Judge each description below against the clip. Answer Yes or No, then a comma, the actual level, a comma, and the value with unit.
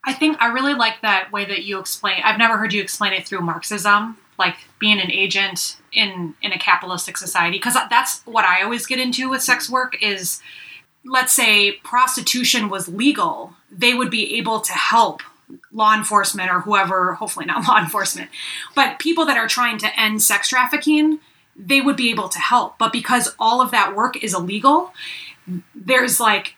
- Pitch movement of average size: Yes, average, 4.4 semitones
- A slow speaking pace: No, average, 185 wpm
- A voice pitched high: Yes, high, 220 Hz